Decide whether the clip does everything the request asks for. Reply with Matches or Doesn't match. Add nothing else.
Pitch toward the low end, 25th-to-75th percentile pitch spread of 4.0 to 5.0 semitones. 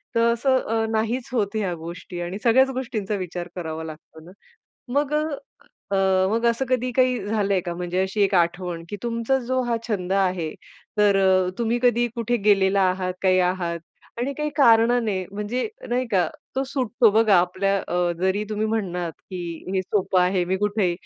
Doesn't match